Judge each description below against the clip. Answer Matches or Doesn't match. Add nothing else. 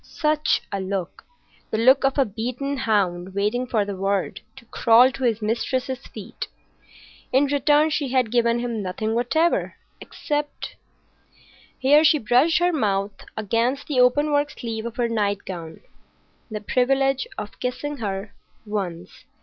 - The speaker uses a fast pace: Doesn't match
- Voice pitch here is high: Matches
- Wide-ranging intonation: Doesn't match